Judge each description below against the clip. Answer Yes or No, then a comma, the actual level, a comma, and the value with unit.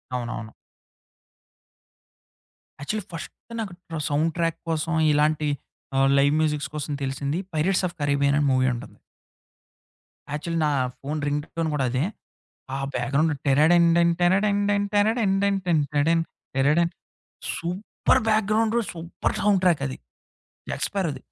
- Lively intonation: No, average, 4.1 semitones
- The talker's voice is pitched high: No, medium, 160 Hz